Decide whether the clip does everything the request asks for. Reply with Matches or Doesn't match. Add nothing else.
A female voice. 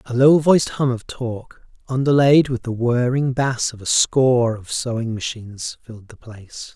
Doesn't match